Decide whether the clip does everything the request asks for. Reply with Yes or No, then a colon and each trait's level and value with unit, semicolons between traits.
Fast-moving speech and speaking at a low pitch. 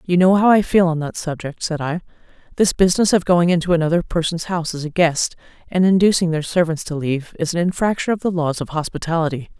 No: fast, 220 wpm; medium, 170 Hz